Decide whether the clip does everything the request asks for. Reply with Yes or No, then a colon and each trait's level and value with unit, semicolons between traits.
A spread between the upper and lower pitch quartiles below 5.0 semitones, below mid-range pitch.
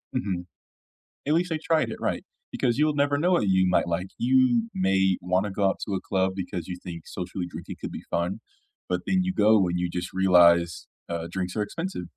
No: wide, 6.0 semitones; very low, 95 Hz